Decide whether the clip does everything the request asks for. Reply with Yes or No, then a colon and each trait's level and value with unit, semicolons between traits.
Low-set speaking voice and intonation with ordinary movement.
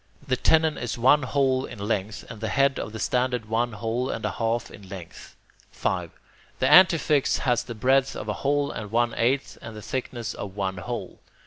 Yes: low, 120 Hz; average, 3.8 semitones